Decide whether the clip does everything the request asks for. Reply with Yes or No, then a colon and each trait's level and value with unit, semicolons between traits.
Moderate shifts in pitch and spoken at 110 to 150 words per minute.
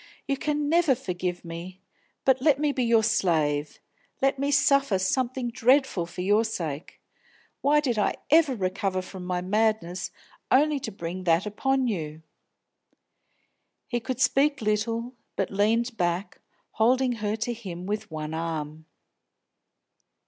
No: wide, 6.6 semitones; average, 140 wpm